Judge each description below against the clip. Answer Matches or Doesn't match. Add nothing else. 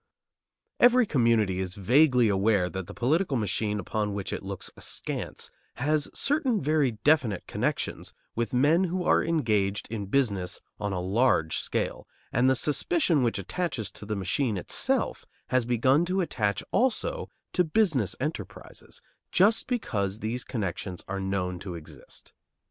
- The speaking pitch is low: Matches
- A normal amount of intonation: Doesn't match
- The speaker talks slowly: Doesn't match